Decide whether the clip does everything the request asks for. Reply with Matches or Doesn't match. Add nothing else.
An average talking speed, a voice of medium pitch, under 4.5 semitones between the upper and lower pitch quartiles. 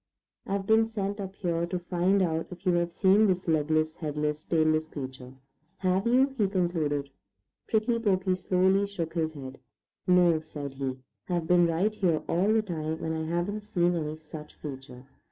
Matches